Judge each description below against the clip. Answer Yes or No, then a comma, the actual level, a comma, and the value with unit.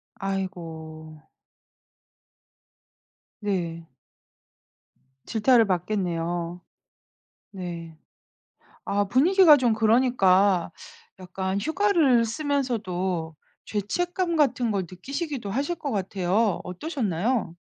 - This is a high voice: Yes, high, 200 Hz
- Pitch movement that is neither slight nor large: No, wide, 6.5 semitones